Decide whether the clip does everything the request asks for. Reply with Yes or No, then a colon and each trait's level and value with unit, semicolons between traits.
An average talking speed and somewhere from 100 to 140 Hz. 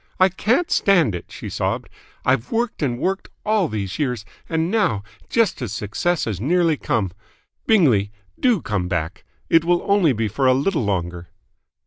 Yes: average, 165 wpm; low, 135 Hz